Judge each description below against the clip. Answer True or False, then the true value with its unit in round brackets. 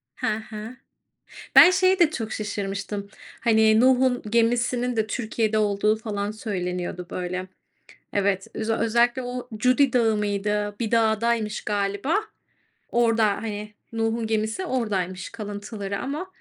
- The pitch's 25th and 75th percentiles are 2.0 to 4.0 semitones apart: True (2.7 semitones)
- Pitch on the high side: True (220 Hz)